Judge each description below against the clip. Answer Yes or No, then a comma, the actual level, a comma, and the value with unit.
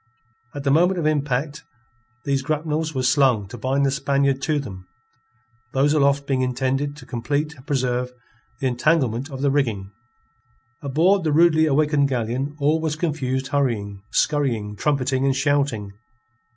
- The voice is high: No, medium, 140 Hz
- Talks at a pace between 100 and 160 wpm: Yes, average, 150 wpm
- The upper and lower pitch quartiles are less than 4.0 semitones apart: Yes, narrow, 2.6 semitones